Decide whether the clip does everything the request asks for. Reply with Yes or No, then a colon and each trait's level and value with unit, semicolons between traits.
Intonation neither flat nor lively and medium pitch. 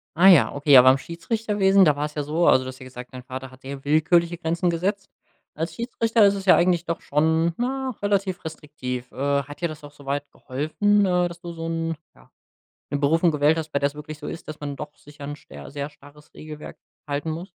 Yes: average, 3.5 semitones; medium, 155 Hz